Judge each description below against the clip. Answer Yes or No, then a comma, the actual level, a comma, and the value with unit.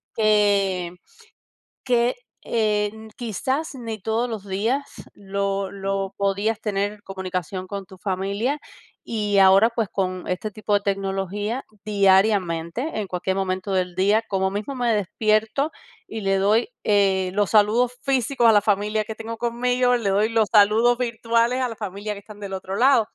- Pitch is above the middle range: Yes, high, 210 Hz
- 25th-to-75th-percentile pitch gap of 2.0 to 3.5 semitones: Yes, average, 2.8 semitones